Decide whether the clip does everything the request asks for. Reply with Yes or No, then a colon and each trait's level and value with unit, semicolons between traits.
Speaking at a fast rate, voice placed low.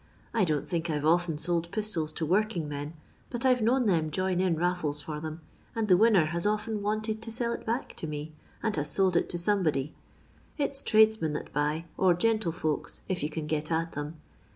No: fast, 210 wpm; medium, 175 Hz